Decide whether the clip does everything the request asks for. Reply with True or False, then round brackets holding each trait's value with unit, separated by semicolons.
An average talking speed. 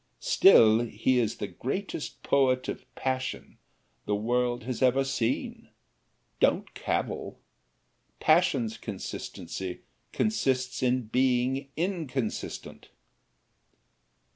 False (90 wpm)